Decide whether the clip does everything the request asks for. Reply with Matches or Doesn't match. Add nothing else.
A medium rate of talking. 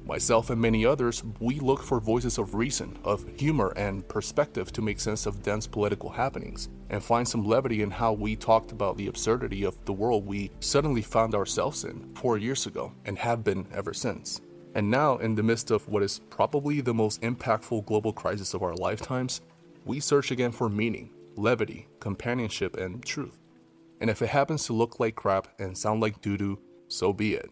Matches